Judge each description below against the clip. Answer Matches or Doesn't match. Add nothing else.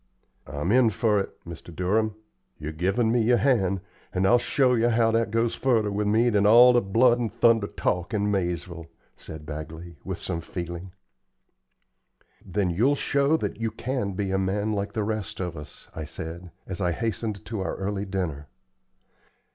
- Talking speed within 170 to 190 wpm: Matches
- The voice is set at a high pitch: Doesn't match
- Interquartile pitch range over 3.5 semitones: Matches